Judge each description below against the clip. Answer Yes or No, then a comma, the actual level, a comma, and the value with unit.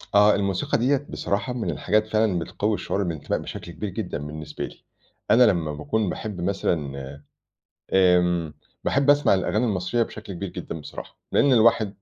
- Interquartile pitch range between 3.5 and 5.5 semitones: Yes, average, 4.1 semitones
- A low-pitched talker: Yes, low, 100 Hz